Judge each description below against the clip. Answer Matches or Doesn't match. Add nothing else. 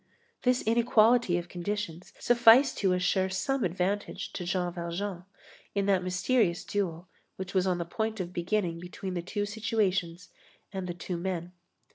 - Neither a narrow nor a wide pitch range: Matches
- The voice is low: Doesn't match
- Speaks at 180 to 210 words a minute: Doesn't match